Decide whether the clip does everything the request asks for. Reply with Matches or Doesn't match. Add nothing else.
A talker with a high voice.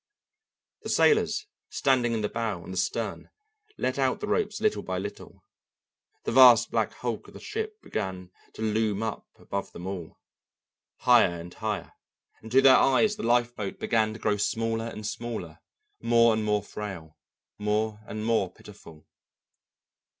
Doesn't match